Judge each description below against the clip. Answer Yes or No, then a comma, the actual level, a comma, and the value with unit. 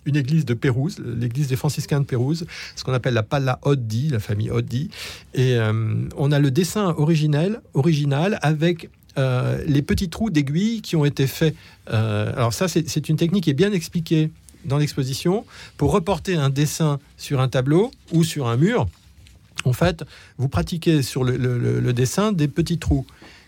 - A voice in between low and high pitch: Yes, medium, 145 Hz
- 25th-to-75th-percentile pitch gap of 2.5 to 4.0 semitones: No, average, 4.7 semitones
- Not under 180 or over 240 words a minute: Yes, average, 185 wpm